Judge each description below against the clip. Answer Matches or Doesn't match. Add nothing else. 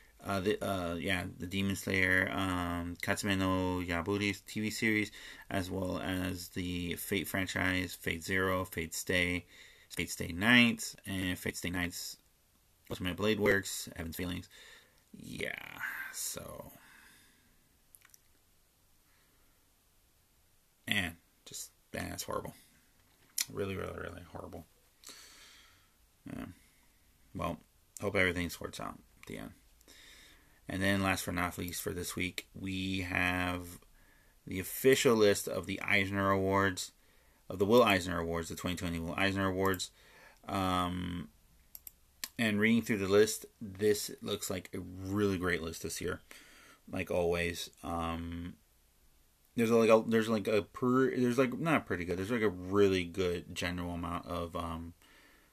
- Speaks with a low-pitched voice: Matches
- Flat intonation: Matches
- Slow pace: Matches